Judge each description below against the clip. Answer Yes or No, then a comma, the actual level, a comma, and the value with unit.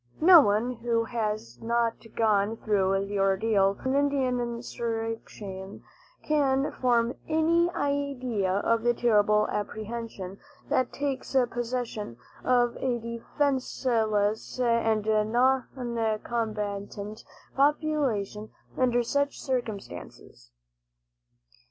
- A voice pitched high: Yes, high, 230 Hz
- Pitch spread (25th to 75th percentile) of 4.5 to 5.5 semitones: No, average, 3.4 semitones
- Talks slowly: Yes, slow, 90 wpm